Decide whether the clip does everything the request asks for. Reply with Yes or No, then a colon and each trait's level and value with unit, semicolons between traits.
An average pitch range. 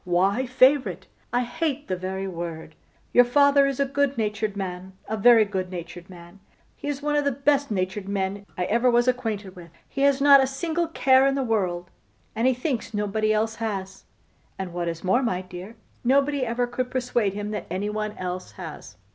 No: wide, 5.7 semitones